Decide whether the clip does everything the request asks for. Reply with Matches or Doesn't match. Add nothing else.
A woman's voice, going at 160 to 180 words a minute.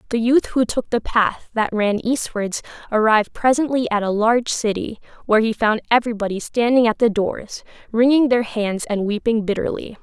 Matches